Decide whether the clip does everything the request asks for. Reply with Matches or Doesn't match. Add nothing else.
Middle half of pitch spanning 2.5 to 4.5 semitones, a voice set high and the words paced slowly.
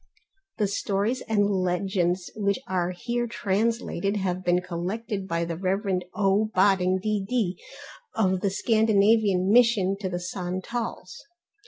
Matches